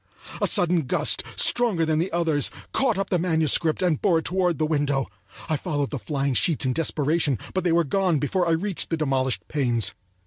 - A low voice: No, medium, 160 Hz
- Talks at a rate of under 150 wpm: No, average, 200 wpm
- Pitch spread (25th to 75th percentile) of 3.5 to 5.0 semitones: Yes, average, 3.8 semitones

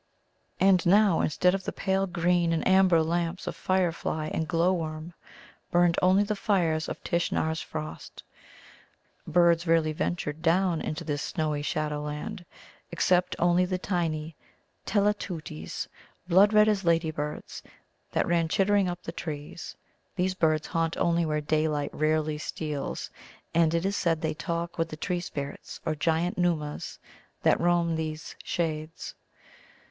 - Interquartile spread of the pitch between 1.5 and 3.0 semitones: Yes, narrow, 2.6 semitones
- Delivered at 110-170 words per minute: Yes, average, 140 wpm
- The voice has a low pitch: No, medium, 170 Hz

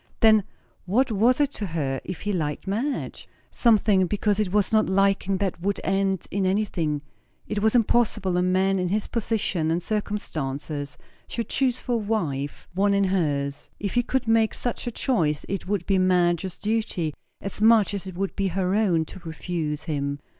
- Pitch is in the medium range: No, high, 195 Hz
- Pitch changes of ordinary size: Yes, average, 3.9 semitones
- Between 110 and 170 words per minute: No, average, 180 wpm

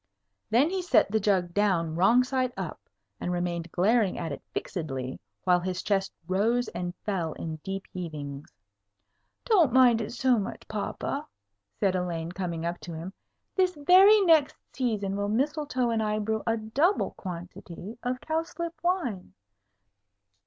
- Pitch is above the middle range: Yes, high, 205 Hz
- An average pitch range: No, wide, 6.4 semitones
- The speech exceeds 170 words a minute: No, average, 150 wpm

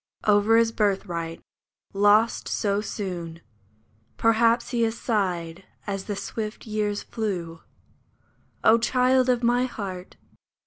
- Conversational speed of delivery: No, slow, 115 wpm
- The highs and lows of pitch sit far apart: No, average, 3.2 semitones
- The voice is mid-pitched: No, high, 210 Hz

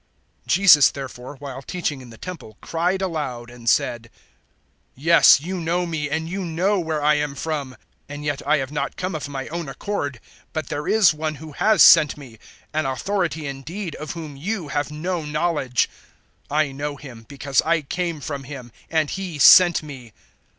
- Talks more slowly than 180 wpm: No, average, 185 wpm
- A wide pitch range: No, average, 3.6 semitones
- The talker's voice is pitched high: No, medium, 150 Hz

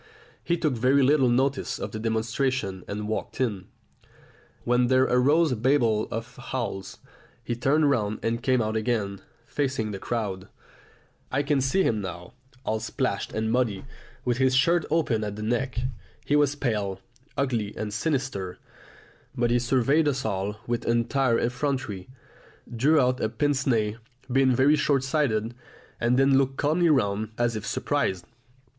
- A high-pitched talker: No, low, 120 Hz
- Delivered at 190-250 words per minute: No, average, 155 wpm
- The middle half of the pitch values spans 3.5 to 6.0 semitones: Yes, average, 3.8 semitones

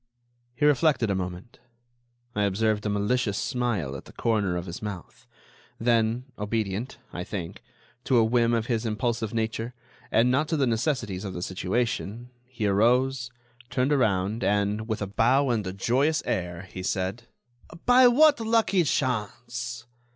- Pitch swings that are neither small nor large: Yes, average, 3.8 semitones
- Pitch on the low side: Yes, low, 115 Hz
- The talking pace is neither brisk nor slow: Yes, average, 155 wpm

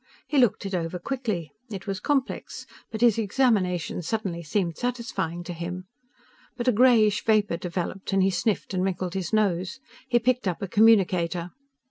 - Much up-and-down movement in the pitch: No, average, 4.2 semitones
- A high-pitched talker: Yes, high, 195 Hz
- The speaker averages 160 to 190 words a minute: Yes, average, 165 wpm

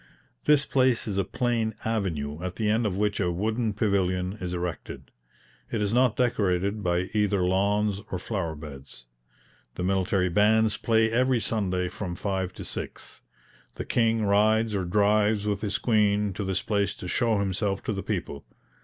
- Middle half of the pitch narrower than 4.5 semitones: Yes, average, 3.1 semitones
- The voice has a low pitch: Yes, low, 100 Hz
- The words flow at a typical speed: Yes, average, 170 wpm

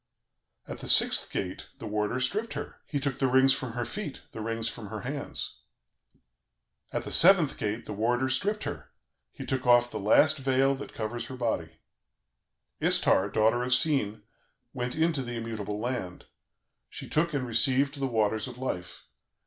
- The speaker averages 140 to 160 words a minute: No, average, 170 wpm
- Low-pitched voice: Yes, low, 125 Hz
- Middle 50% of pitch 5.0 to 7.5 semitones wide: No, average, 3.6 semitones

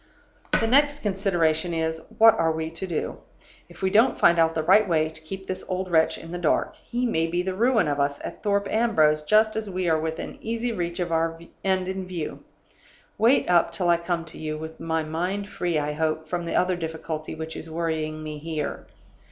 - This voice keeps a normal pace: No, fast, 215 wpm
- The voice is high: No, medium, 170 Hz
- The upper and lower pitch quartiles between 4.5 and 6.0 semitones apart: No, average, 3.2 semitones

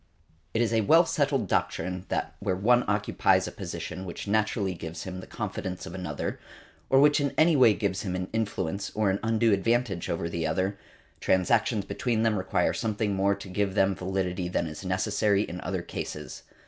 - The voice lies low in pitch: Yes, low, 100 Hz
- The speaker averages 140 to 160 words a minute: No, average, 185 wpm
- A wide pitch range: No, average, 3.3 semitones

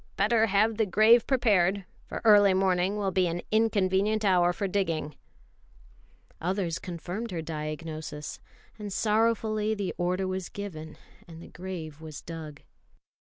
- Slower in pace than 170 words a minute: Yes, slow, 135 wpm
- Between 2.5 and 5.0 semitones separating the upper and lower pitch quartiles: Yes, average, 4.0 semitones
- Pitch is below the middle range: No, high, 190 Hz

